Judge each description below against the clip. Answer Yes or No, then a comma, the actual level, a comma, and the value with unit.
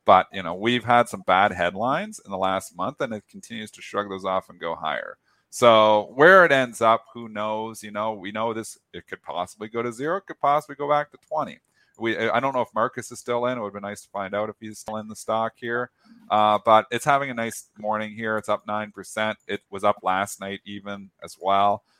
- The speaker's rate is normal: No, fast, 245 wpm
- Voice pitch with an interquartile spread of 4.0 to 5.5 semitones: No, average, 2.9 semitones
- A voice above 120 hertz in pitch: No, low, 110 Hz